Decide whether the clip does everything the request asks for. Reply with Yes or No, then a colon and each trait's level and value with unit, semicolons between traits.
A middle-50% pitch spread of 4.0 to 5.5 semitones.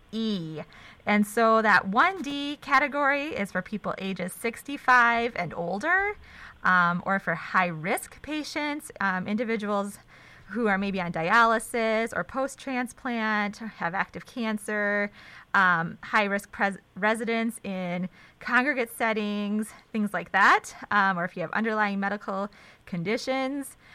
Yes: average, 4.3 semitones